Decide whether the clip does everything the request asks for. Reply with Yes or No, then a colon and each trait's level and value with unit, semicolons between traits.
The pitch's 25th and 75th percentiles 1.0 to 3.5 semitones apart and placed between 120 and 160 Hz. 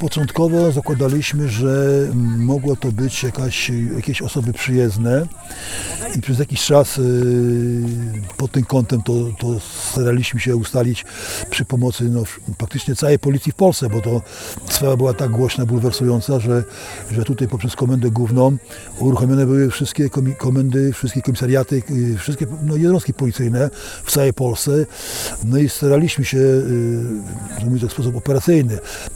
Yes: narrow, 2.4 semitones; low, 130 Hz